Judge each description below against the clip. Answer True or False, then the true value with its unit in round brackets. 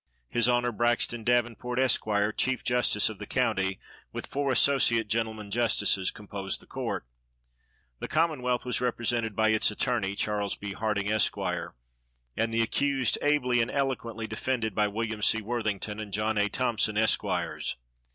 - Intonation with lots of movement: False (2.7 semitones)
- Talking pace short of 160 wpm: True (150 wpm)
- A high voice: False (115 Hz)